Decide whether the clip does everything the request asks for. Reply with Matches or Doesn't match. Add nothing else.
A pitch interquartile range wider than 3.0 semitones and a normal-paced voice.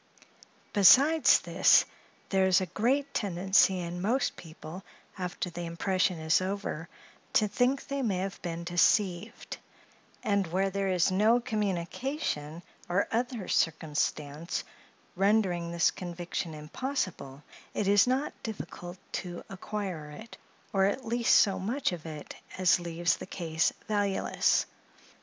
Doesn't match